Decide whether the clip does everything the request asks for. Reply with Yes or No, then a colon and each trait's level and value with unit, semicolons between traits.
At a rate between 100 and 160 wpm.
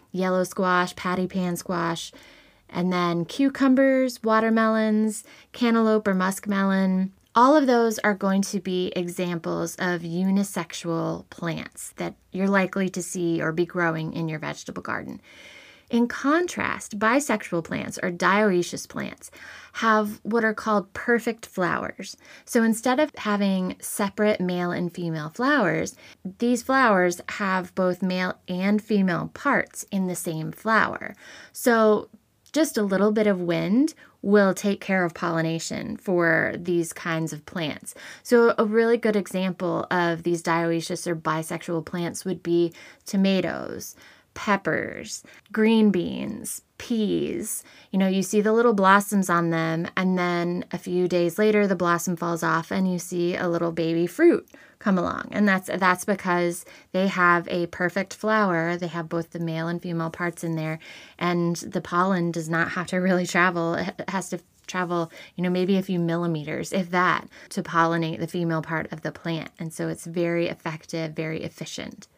Yes: average, 155 wpm